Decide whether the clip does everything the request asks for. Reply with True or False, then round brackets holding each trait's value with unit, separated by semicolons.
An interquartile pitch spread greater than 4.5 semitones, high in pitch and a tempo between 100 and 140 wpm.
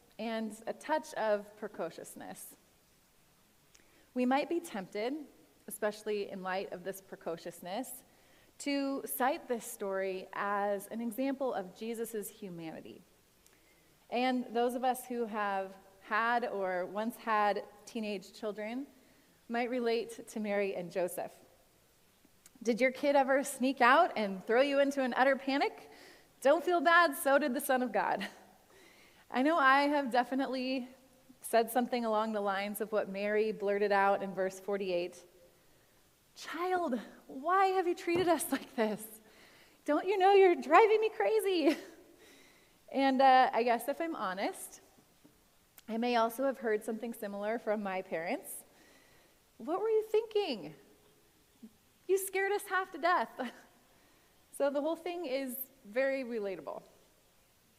True (5.1 semitones; 240 Hz; 135 wpm)